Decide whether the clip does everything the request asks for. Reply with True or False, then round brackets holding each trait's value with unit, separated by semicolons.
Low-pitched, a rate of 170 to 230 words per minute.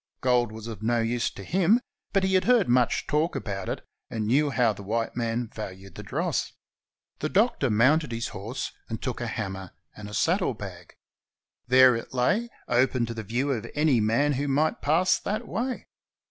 True (120 Hz; 190 wpm)